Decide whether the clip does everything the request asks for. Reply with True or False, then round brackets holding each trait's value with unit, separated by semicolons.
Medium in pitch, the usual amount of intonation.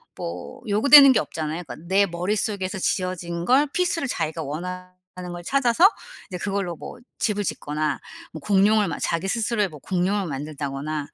True (180 Hz; 4.6 semitones)